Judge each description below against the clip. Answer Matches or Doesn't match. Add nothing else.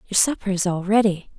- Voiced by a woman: Matches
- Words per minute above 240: Doesn't match